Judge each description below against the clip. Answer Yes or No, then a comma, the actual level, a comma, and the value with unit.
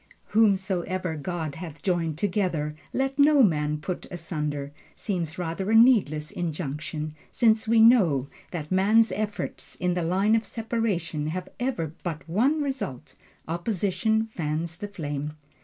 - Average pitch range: No, wide, 5.7 semitones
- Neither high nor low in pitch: Yes, medium, 180 Hz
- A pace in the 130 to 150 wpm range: Yes, slow, 135 wpm